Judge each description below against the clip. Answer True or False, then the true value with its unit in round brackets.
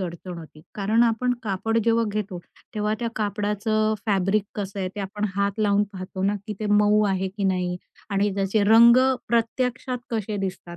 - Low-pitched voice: False (205 Hz)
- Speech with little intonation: True (2.1 semitones)